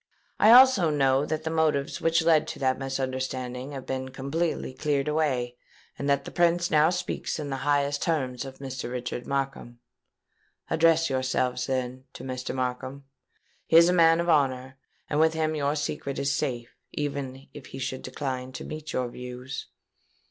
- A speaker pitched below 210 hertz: Yes, medium, 140 Hz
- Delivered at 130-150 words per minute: No, average, 170 wpm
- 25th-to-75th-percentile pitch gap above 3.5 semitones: No, average, 3.2 semitones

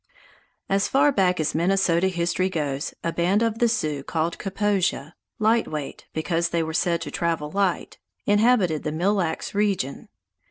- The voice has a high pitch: No, medium, 175 Hz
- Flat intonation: No, average, 3.9 semitones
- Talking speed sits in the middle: Yes, average, 160 wpm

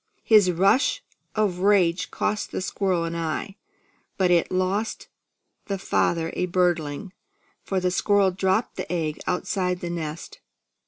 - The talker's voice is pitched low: No, medium, 180 Hz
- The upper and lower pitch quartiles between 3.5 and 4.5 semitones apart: No, narrow, 2.5 semitones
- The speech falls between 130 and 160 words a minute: Yes, average, 140 wpm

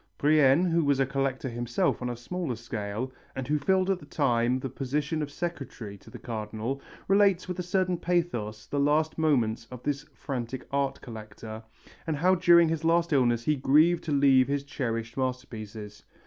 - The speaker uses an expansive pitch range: No, average, 5.0 semitones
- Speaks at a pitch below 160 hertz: Yes, low, 135 Hz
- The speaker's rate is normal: Yes, average, 185 wpm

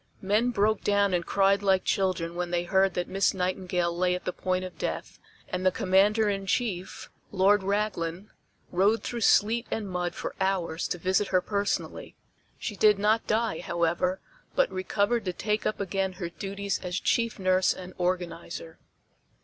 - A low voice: No, high, 190 Hz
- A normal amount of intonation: No, narrow, 2.2 semitones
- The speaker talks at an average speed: Yes, average, 170 wpm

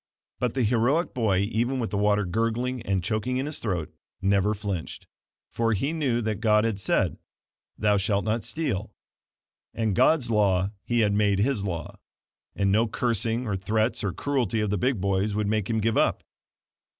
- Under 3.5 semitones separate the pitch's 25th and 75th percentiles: Yes, average, 2.8 semitones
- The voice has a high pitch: No, low, 110 Hz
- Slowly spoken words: No, average, 180 wpm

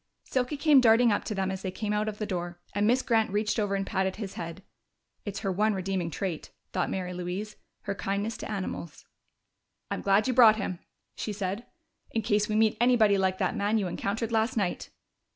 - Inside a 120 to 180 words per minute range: No, fast, 205 wpm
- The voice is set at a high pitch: Yes, high, 205 Hz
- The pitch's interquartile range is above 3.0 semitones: No, narrow, 2.6 semitones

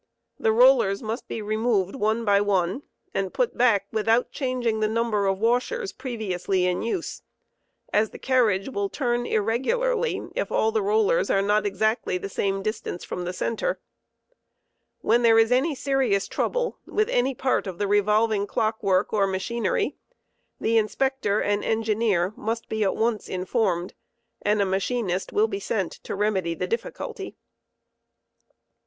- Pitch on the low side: No, high, 220 Hz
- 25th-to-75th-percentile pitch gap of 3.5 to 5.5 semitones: Yes, average, 3.8 semitones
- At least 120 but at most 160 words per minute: Yes, average, 155 wpm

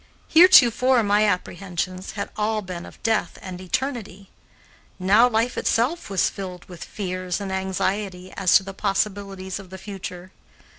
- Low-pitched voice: No, high, 195 Hz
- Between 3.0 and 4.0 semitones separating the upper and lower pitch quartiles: No, narrow, 2.6 semitones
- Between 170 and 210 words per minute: No, average, 145 wpm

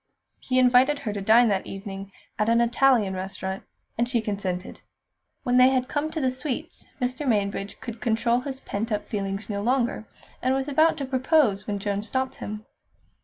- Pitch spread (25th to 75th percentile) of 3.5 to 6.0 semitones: Yes, average, 4.4 semitones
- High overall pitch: Yes, high, 235 Hz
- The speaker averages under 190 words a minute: Yes, average, 180 wpm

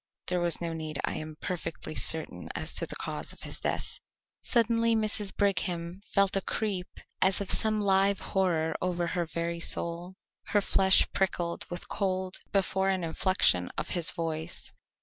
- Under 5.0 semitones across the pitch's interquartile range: Yes, narrow, 2.6 semitones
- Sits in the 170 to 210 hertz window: Yes, medium, 185 Hz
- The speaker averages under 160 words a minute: No, average, 165 wpm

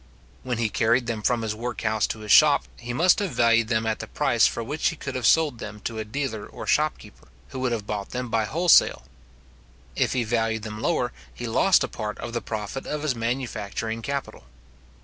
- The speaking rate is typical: No, fast, 210 wpm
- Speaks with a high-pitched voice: No, low, 115 Hz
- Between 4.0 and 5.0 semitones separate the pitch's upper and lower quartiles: No, average, 2.8 semitones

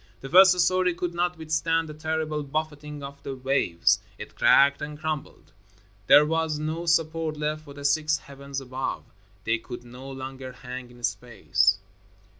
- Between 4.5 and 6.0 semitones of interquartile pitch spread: No, average, 3.1 semitones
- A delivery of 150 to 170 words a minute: Yes, average, 160 wpm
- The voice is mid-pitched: Yes, medium, 150 Hz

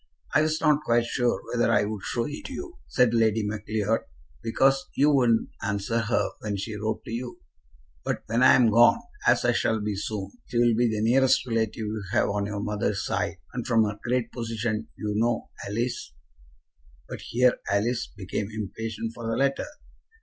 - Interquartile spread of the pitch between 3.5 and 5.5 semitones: No, narrow, 2.5 semitones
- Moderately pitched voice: No, low, 115 Hz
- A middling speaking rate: Yes, average, 180 wpm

